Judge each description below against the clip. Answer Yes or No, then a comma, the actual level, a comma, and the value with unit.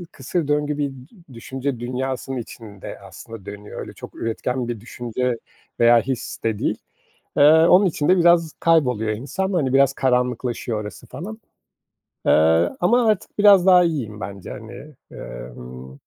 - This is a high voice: No, low, 130 Hz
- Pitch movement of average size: No, wide, 6.1 semitones